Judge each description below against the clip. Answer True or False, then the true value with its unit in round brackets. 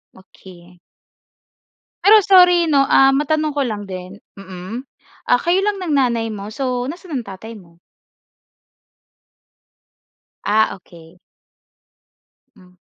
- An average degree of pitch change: False (8.4 semitones)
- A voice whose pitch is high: True (230 Hz)